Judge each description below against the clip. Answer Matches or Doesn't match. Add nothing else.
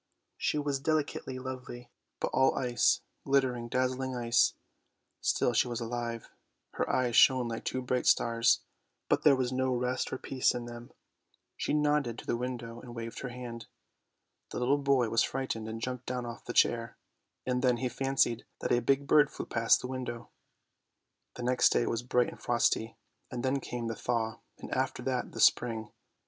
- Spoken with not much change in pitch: Matches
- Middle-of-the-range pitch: Doesn't match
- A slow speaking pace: Doesn't match